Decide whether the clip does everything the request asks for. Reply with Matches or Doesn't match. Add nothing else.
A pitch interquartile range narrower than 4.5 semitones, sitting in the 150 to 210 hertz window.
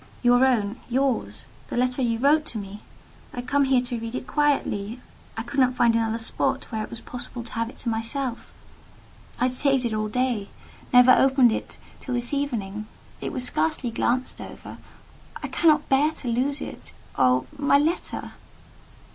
Doesn't match